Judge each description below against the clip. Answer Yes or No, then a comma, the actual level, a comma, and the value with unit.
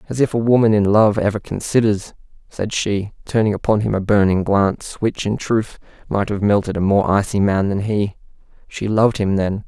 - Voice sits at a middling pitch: No, low, 105 Hz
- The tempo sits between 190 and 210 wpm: Yes, average, 200 wpm